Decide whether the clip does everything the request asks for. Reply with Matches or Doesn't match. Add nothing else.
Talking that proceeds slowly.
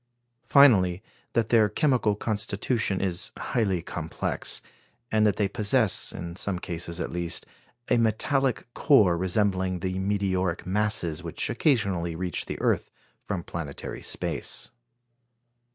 Matches